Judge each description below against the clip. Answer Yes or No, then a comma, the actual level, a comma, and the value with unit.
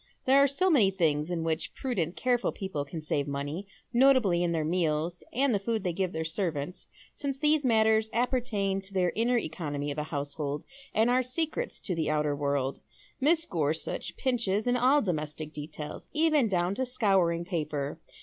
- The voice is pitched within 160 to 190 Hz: Yes, medium, 185 Hz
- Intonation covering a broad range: Yes, wide, 8.1 semitones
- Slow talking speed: No, average, 180 wpm